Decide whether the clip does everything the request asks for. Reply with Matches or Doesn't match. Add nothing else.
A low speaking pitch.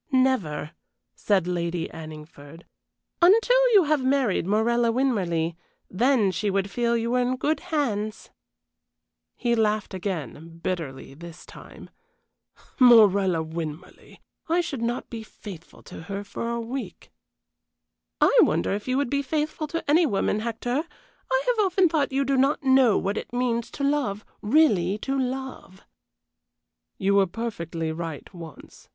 Doesn't match